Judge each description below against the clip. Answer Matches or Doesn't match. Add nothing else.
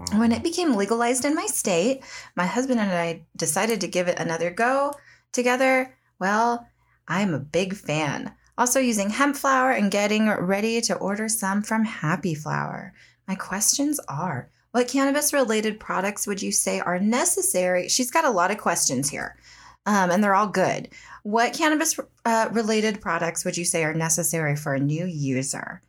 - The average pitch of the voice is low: Doesn't match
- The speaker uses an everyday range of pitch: Doesn't match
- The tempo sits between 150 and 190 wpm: Matches